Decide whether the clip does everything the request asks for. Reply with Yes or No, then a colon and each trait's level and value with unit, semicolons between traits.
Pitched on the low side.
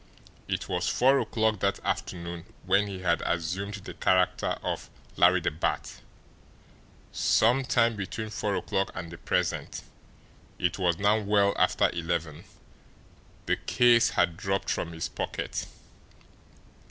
Yes: very low, 95 Hz